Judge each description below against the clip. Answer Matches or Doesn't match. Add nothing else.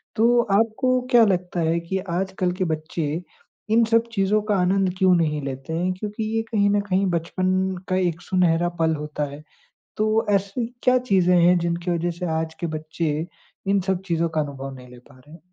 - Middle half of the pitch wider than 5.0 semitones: Doesn't match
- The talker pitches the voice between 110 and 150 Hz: Doesn't match